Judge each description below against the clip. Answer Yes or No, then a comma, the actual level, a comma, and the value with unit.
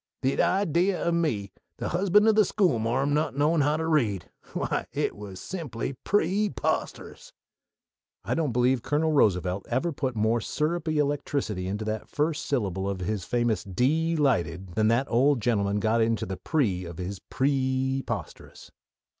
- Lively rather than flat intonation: Yes, wide, 6.9 semitones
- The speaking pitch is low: Yes, low, 130 Hz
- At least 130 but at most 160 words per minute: Yes, average, 155 wpm